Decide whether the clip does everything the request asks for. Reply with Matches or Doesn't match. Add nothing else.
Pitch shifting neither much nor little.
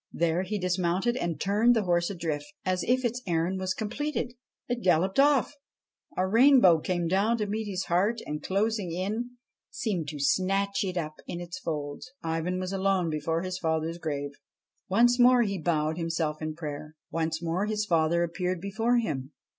Matches